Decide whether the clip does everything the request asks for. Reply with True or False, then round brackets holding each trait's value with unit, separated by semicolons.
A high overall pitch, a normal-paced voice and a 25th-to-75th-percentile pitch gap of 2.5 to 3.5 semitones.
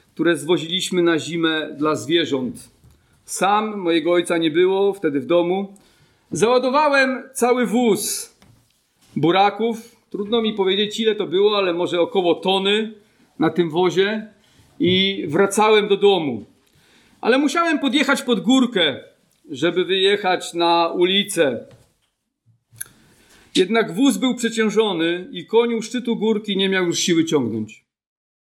False (195 Hz; 120 wpm; 4.8 semitones)